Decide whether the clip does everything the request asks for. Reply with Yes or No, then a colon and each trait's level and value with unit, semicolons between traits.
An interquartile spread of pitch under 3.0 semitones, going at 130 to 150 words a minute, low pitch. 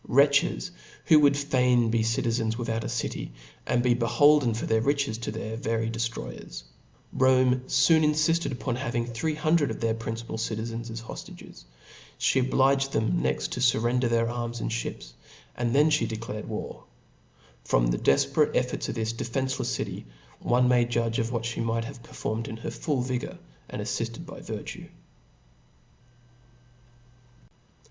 No: narrow, 2.6 semitones; average, 165 wpm; low, 120 Hz